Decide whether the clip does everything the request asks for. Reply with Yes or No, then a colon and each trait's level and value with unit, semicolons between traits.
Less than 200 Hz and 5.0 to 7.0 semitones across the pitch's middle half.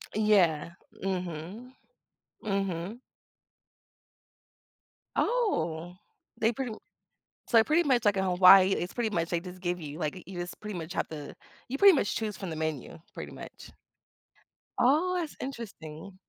Yes: high, 190 Hz; average, 5.3 semitones